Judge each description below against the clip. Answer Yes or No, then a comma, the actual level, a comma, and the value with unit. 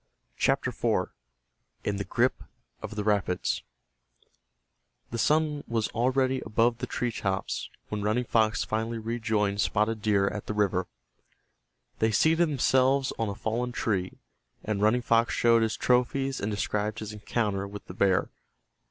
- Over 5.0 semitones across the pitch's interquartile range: No, average, 2.9 semitones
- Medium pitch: No, low, 110 Hz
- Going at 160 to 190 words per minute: No, average, 145 wpm